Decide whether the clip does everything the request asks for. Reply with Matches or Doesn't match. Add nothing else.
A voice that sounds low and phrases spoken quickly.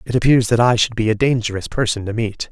Matches